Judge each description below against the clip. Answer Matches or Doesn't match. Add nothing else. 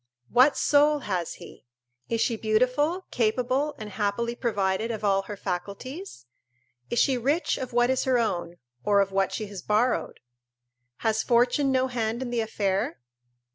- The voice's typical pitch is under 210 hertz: Doesn't match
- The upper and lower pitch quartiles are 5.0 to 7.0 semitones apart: Doesn't match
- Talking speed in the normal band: Matches